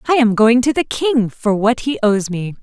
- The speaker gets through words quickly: Yes, fast, 250 wpm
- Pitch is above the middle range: Yes, high, 235 Hz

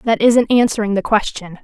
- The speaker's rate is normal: Yes, average, 185 wpm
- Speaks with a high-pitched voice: Yes, high, 215 Hz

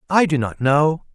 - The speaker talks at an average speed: No, fast, 210 wpm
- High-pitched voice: No, medium, 150 Hz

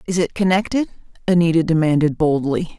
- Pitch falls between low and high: Yes, medium, 170 Hz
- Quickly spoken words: No, slow, 130 wpm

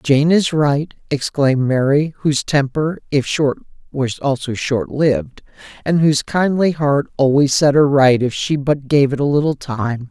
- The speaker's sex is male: Yes, male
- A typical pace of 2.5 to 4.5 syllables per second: Yes, 4.4 syllables/s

